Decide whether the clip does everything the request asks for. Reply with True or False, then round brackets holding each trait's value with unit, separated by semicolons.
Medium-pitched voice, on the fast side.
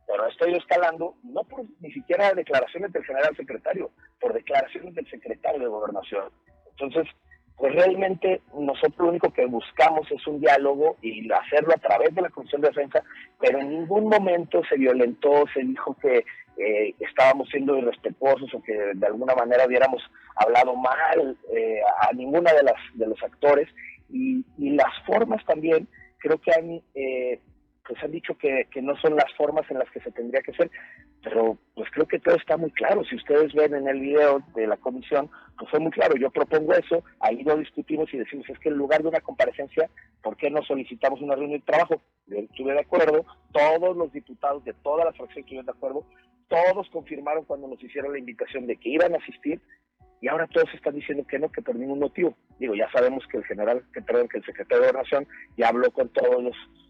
True (155 Hz; 200 wpm)